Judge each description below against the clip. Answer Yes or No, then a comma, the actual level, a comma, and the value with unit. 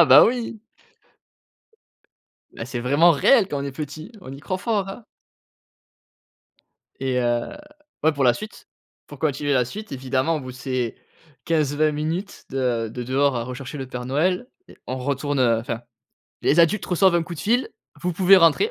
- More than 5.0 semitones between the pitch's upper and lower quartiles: Yes, wide, 5.6 semitones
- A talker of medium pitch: Yes, medium, 145 Hz